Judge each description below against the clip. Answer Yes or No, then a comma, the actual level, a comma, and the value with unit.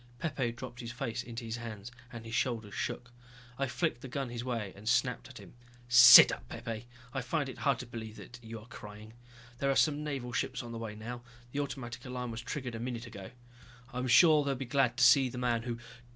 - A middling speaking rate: No, fast, 235 wpm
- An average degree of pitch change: No, narrow, 2.0 semitones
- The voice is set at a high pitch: No, low, 120 Hz